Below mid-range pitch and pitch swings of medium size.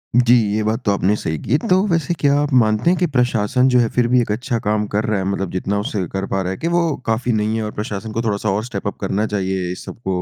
Yes: low, 110 Hz; average, 3.7 semitones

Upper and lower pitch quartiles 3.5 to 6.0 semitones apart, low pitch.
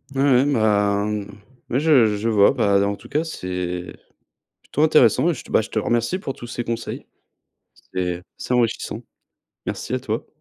Yes: average, 4.4 semitones; low, 115 Hz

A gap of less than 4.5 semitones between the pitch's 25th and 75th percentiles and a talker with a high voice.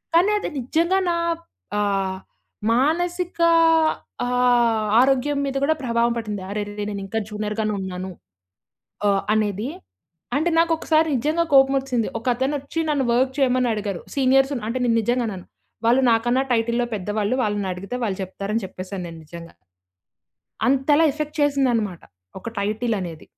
No: average, 4.8 semitones; high, 235 Hz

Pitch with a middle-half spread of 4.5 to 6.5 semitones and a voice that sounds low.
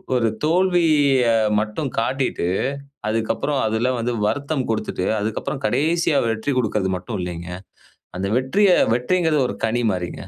Yes: wide, 5.5 semitones; low, 125 Hz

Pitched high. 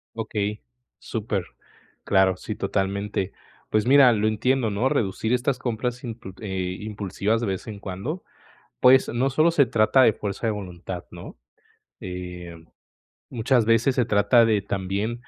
No: low, 110 Hz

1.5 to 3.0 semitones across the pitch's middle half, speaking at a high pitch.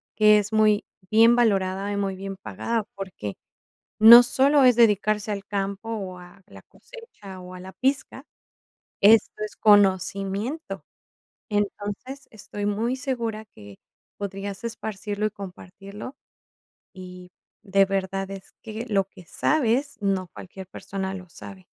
Yes: narrow, 2.6 semitones; high, 205 Hz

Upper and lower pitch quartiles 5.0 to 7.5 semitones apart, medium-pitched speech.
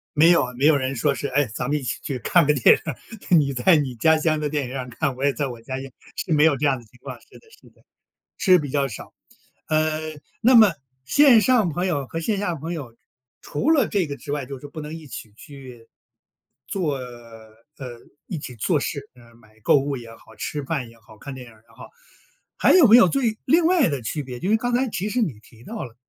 Yes: wide, 5.5 semitones; medium, 145 Hz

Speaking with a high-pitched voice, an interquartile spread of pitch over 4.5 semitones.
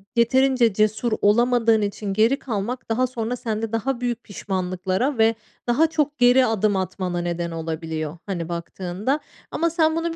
Yes: high, 225 Hz; average, 5.0 semitones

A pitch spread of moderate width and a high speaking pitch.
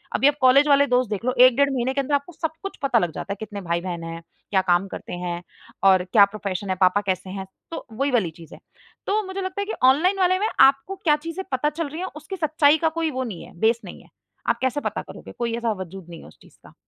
No: wide, 7.7 semitones; very high, 255 Hz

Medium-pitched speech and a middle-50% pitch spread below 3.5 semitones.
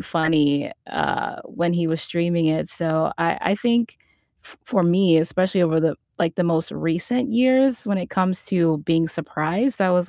Yes: medium, 170 Hz; average, 2.9 semitones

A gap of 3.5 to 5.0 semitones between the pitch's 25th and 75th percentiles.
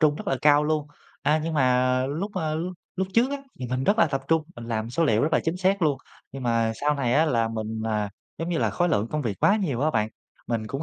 No: wide, 5.5 semitones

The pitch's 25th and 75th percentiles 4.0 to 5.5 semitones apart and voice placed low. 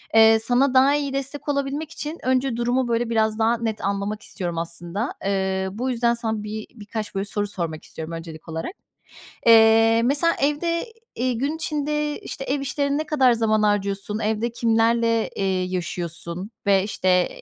No: average, 5.2 semitones; high, 225 Hz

